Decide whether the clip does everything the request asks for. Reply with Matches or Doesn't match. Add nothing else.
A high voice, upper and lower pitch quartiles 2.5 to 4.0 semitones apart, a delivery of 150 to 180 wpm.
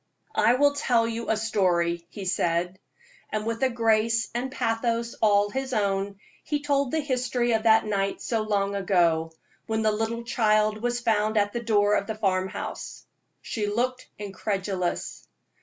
Matches